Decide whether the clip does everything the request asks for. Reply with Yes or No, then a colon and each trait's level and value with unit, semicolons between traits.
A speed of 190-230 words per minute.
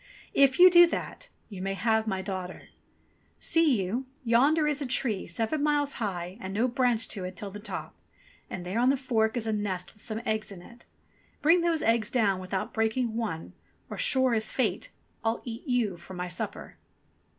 Yes: average, 195 wpm